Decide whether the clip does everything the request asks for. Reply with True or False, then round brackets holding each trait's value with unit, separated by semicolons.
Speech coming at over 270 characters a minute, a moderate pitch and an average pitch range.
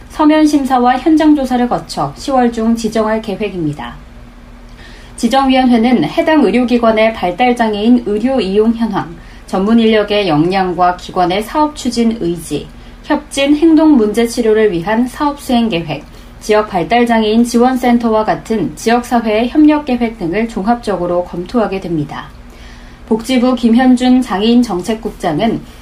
False (305 characters per minute; 225 Hz; 4.6 semitones)